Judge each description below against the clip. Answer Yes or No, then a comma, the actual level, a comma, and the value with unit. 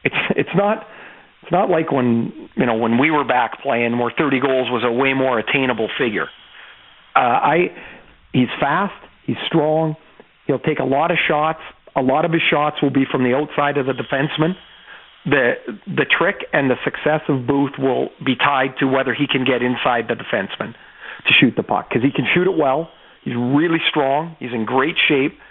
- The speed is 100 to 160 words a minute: No, average, 200 wpm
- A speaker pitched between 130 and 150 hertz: Yes, medium, 140 Hz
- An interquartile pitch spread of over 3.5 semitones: No, average, 3.1 semitones